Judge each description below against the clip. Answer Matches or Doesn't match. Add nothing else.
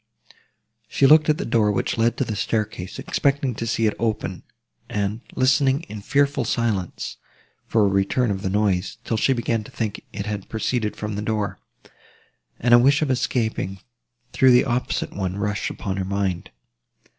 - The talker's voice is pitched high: Doesn't match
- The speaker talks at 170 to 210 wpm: Matches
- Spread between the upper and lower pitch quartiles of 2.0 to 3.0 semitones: Doesn't match